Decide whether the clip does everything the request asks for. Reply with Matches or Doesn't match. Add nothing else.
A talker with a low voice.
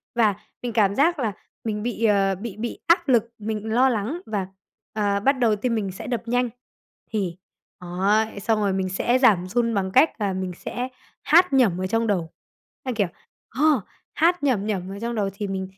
Doesn't match